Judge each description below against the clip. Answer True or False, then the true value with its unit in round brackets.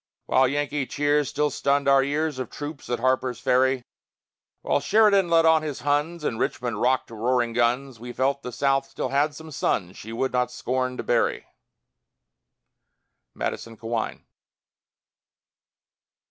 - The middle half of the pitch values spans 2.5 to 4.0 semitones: True (2.9 semitones)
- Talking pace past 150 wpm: False (145 wpm)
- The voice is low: True (130 Hz)